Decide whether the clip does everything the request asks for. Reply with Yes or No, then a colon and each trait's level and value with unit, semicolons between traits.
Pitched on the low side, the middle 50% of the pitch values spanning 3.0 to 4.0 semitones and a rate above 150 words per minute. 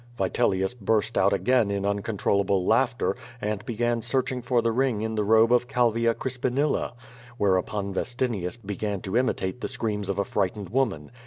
Yes: low, 110 Hz; average, 3.5 semitones; average, 160 wpm